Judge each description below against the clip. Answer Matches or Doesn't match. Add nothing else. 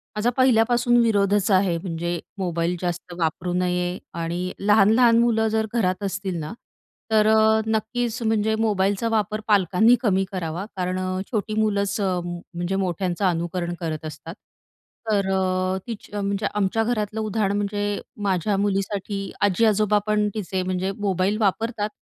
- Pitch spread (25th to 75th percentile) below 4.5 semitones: Matches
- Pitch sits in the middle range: Doesn't match